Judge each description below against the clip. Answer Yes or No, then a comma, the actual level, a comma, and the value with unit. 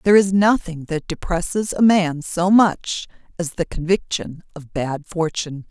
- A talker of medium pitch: Yes, medium, 175 Hz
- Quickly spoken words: No, average, 160 wpm